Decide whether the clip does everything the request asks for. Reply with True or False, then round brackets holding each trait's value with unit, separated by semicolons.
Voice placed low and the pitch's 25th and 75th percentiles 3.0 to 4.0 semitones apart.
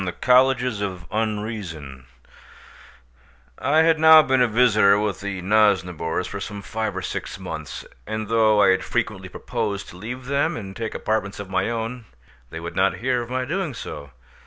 False (110 Hz; 4.4 semitones)